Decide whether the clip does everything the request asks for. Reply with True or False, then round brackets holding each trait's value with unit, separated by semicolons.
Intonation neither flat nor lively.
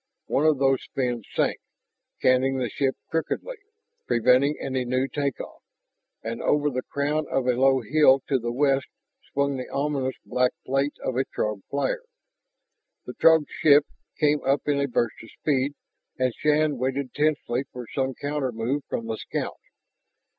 False (2.3 semitones)